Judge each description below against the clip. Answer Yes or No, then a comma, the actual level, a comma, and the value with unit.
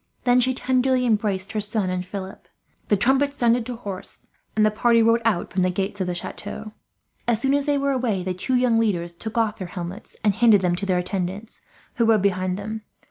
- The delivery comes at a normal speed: No, fast, 220 wpm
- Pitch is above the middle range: Yes, high, 215 Hz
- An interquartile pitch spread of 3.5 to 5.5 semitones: Yes, average, 4.1 semitones